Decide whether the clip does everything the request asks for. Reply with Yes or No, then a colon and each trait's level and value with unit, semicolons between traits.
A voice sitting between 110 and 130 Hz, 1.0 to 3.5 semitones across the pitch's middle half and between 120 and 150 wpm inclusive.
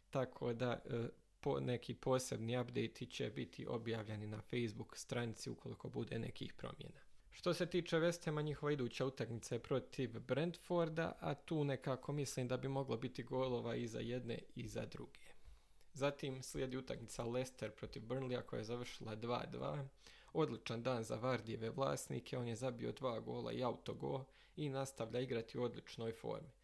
No: low, 125 Hz; average, 2.9 semitones; fast, 160 wpm